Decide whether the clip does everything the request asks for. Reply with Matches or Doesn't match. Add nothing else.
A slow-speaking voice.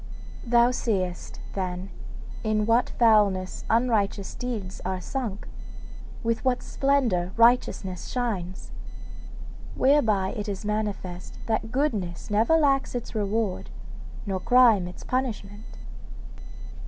Matches